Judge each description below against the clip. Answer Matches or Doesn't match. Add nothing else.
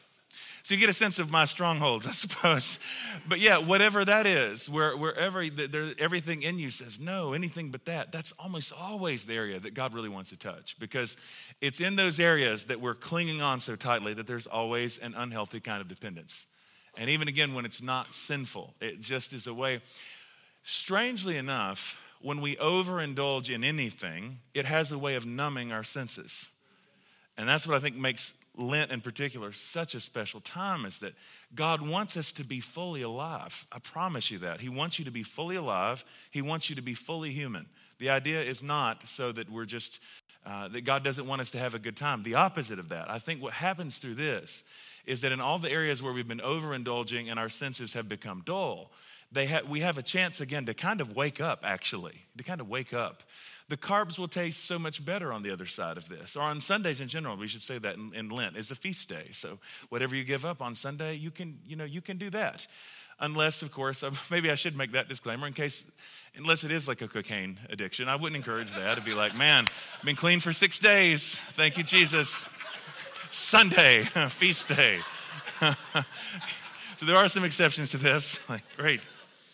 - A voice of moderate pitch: Matches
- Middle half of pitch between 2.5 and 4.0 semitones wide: Doesn't match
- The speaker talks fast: Matches